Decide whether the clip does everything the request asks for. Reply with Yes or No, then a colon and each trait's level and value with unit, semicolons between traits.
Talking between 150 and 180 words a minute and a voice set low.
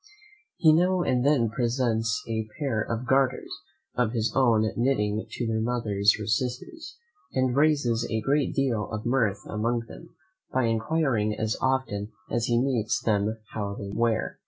Yes: average, 155 wpm; low, 115 Hz